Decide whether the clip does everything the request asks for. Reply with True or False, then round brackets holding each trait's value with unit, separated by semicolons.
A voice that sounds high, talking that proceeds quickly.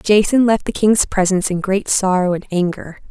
False (195 Hz; 195 wpm)